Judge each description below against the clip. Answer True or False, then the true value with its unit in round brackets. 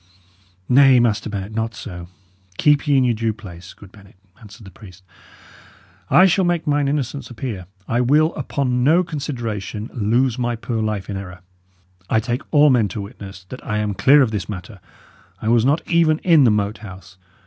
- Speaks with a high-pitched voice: False (115 Hz)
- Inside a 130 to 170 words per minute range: False (185 wpm)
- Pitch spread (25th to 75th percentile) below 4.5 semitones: False (5.2 semitones)